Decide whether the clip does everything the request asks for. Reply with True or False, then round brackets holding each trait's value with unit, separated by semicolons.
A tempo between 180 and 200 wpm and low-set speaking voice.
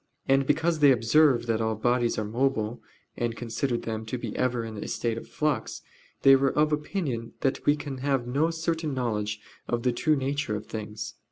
True (195 wpm; 125 Hz)